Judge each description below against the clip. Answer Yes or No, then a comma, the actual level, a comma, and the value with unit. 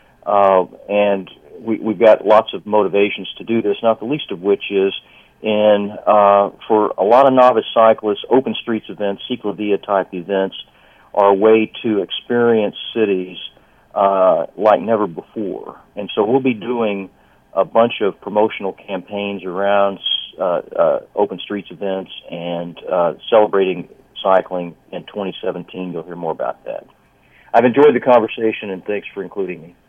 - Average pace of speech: Yes, average, 155 wpm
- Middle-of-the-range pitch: No, low, 100 Hz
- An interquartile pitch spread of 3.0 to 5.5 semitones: No, narrow, 2.6 semitones